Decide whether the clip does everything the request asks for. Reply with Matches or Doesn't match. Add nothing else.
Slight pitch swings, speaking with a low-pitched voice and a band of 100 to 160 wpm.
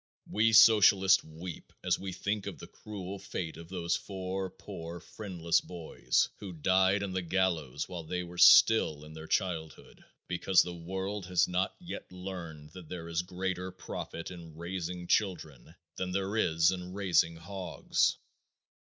Matches